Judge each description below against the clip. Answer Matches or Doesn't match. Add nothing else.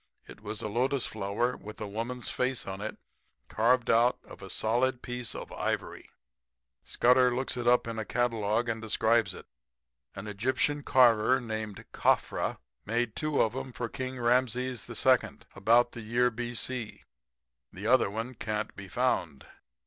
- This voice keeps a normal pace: Matches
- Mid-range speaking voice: Doesn't match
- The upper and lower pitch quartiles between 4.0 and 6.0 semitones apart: Doesn't match